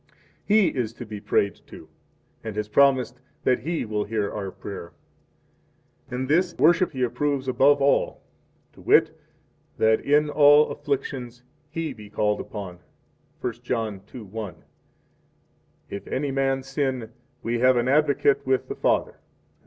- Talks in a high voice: No, low, 125 Hz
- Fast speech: No, average, 150 wpm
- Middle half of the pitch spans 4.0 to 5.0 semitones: Yes, average, 4.5 semitones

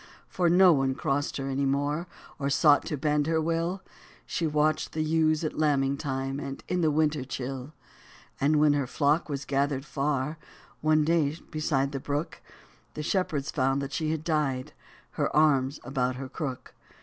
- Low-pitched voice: No, medium, 145 Hz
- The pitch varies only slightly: Yes, narrow, 2.3 semitones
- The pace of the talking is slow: No, average, 175 wpm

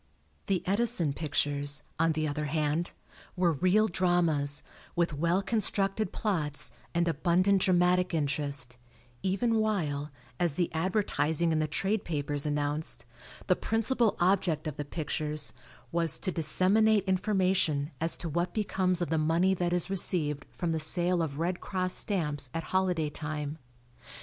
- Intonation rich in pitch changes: No, average, 3.8 semitones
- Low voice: No, medium, 170 Hz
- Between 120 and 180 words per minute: Yes, average, 145 wpm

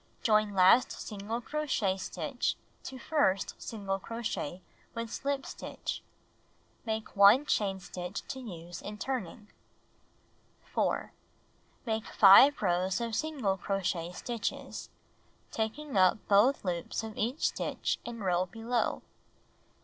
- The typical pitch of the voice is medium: No, high, 215 Hz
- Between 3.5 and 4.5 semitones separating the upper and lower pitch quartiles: Yes, average, 3.9 semitones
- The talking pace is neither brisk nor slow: No, slow, 120 wpm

